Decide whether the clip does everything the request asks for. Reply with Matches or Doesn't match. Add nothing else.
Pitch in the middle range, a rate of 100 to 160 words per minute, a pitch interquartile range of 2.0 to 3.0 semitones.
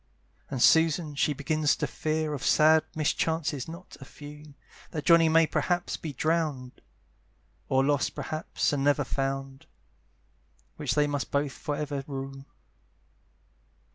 Matches